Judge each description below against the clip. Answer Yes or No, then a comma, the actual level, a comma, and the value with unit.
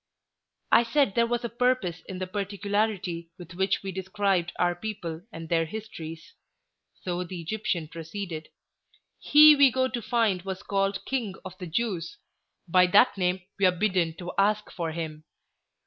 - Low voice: No, high, 190 Hz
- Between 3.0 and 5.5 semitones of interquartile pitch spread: Yes, average, 3.9 semitones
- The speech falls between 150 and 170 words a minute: Yes, average, 165 wpm